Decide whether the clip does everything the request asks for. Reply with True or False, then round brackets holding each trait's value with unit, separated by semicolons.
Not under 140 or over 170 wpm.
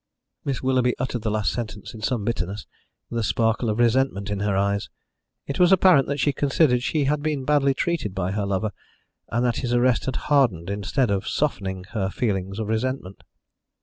False (190 wpm)